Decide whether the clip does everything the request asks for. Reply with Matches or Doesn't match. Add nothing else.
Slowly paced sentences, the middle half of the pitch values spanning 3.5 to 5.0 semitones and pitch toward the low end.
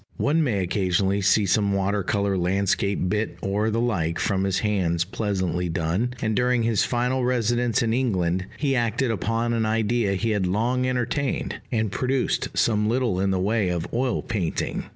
Doesn't match